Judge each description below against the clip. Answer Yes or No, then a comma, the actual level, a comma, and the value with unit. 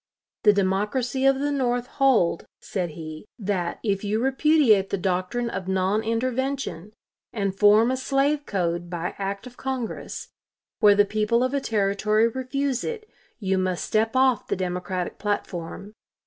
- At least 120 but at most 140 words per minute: No, average, 150 wpm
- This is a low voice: No, high, 215 Hz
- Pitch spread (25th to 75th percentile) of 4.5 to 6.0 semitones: Yes, average, 5.2 semitones